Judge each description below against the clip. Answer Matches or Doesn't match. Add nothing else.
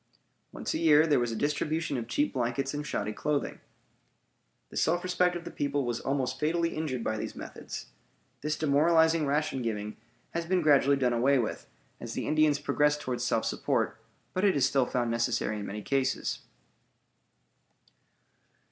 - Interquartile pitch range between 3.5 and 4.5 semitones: Matches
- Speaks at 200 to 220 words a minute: Doesn't match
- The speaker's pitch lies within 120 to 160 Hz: Matches